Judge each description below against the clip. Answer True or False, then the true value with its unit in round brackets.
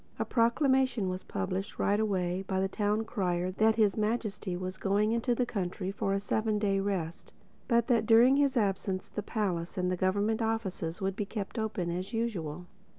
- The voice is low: False (205 Hz)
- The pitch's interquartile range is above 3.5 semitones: False (3.2 semitones)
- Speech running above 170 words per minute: True (185 wpm)